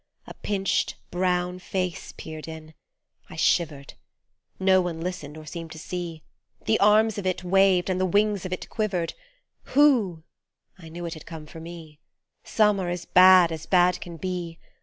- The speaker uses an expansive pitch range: No, narrow, 2.4 semitones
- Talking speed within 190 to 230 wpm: No, average, 170 wpm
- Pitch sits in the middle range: Yes, medium, 180 Hz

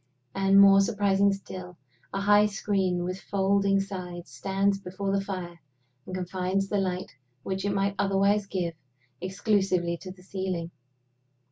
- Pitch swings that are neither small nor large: No, narrow, 1.4 semitones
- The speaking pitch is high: Yes, high, 195 Hz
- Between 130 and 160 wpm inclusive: Yes, average, 140 wpm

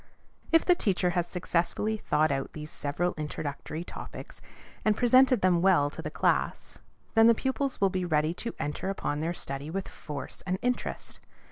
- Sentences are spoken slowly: No, average, 170 wpm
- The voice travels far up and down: Yes, wide, 6.1 semitones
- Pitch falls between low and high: Yes, medium, 175 Hz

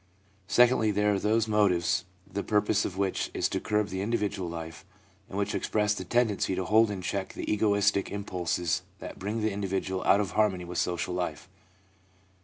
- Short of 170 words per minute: No, average, 180 wpm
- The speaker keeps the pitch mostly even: Yes, narrow, 2.3 semitones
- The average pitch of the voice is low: Yes, low, 100 Hz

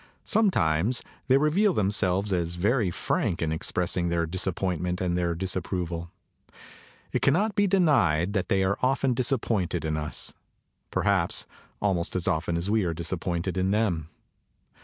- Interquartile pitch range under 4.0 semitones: No, average, 4.8 semitones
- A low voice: Yes, very low, 95 Hz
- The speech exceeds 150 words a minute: No, average, 145 wpm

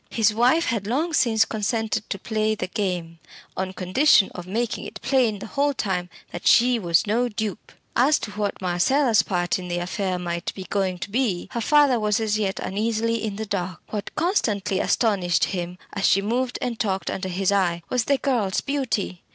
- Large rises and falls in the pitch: No, average, 4.0 semitones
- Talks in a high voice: Yes, high, 210 Hz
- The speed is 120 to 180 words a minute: No, average, 190 wpm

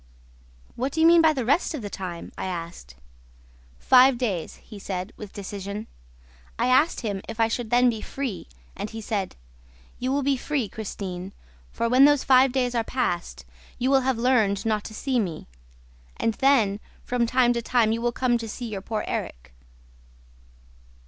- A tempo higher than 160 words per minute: Yes, average, 180 wpm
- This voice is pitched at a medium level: No, high, 230 Hz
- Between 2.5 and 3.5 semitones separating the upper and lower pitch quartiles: No, average, 4.2 semitones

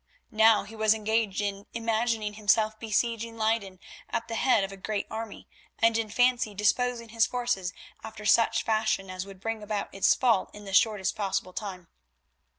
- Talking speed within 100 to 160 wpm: No, average, 170 wpm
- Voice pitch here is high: Yes, high, 215 Hz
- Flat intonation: Yes, narrow, 2.2 semitones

